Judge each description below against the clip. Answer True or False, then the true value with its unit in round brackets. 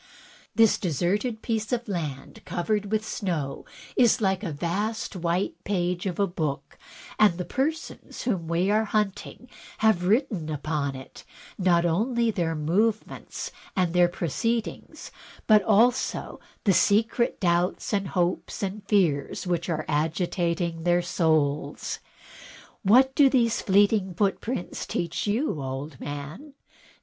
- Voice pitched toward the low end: False (185 Hz)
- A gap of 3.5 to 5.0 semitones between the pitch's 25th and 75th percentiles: True (4.4 semitones)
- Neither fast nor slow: False (130 wpm)